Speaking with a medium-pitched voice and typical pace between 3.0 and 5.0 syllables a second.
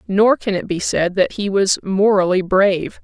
No: high, 195 Hz; 4.6 syllables/s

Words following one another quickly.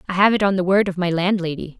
Yes: fast, 300 wpm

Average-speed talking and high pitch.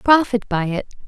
Yes: average, 165 wpm; high, 220 Hz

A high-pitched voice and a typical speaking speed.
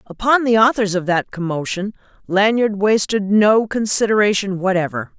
No: high, 205 Hz; slow, 125 wpm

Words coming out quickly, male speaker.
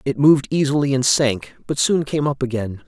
Yes: fast, 210 wpm; male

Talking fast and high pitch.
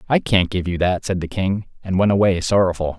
No: fast, 240 wpm; very low, 95 Hz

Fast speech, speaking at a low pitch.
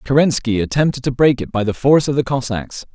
Yes: fast, 225 wpm; low, 125 Hz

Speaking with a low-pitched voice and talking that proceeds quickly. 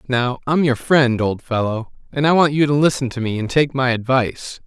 Yes: low, 130 Hz; fast, 230 wpm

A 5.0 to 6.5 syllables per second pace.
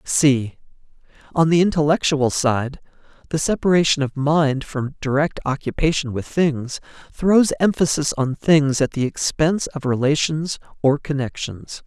No: 4.6 syllables/s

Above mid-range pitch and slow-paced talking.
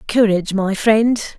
Yes: high, 210 Hz; slow, 130 wpm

